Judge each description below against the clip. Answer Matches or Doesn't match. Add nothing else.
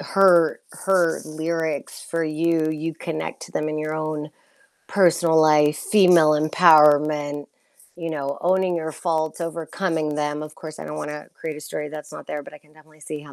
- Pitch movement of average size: Doesn't match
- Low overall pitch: Doesn't match